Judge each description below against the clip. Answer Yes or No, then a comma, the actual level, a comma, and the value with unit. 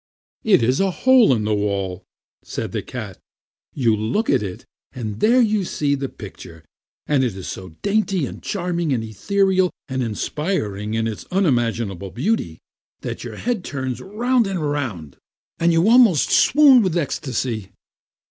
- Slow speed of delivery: No, average, 155 wpm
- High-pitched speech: No, medium, 140 Hz